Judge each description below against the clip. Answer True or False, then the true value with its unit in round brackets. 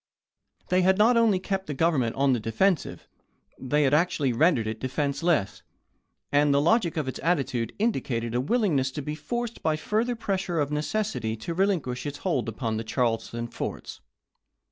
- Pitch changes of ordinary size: False (7.1 semitones)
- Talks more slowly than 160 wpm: False (165 wpm)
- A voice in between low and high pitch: True (150 Hz)